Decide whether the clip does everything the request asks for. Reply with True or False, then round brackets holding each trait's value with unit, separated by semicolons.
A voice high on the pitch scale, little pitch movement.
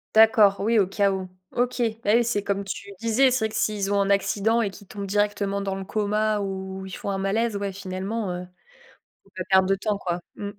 True (200 Hz; 1.8 semitones)